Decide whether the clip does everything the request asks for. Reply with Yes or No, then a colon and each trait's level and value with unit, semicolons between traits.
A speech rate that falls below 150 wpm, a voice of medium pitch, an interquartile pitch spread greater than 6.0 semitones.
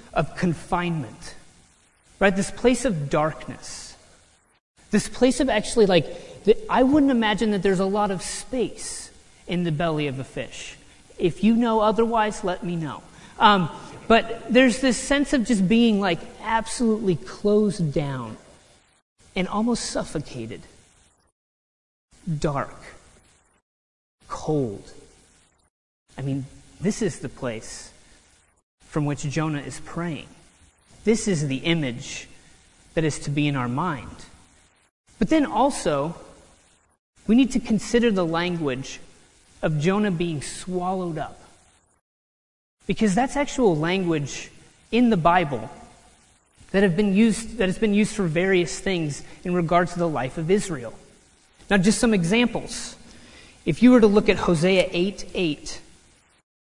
Yes: slow, 135 wpm; medium, 175 Hz; wide, 8.3 semitones